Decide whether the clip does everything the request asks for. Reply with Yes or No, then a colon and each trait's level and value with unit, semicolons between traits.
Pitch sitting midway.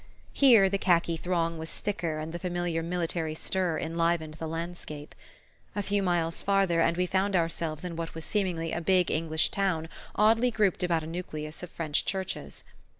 Yes: medium, 170 Hz